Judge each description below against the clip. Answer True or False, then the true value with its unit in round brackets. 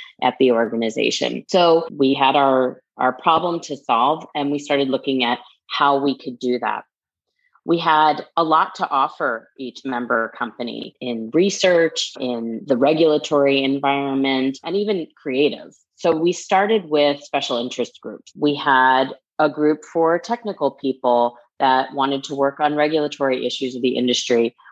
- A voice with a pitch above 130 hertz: True (140 Hz)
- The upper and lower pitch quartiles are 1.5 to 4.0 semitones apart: True (3.7 semitones)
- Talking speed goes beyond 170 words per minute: False (155 wpm)